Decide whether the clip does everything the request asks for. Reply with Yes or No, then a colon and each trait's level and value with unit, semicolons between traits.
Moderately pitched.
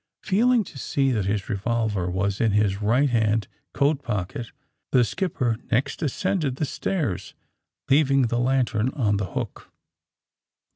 No: low, 120 Hz